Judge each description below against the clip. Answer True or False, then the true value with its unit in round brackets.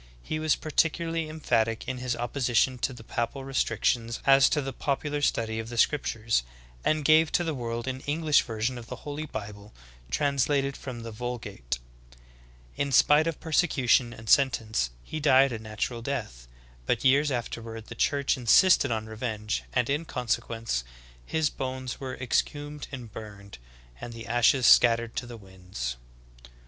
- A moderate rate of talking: True (160 wpm)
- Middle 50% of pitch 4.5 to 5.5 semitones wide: False (4.0 semitones)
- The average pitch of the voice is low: True (125 Hz)